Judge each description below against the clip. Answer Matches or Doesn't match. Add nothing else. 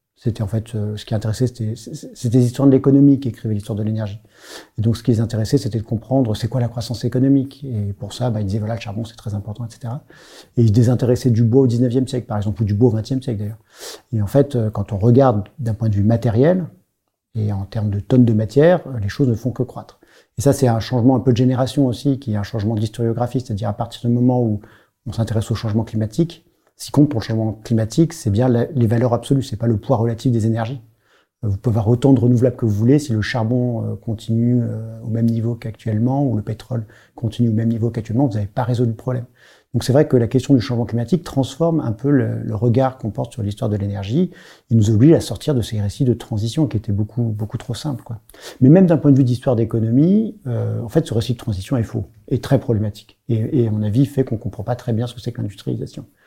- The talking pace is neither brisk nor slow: Doesn't match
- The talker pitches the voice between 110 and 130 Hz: Matches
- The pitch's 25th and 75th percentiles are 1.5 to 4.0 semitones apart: Matches